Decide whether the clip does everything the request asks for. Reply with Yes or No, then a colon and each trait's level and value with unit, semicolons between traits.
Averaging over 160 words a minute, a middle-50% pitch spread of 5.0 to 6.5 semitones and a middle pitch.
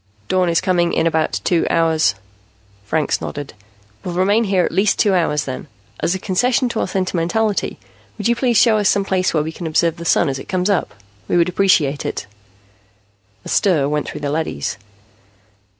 No: average, 185 wpm; average, 3.8 semitones; medium, 175 Hz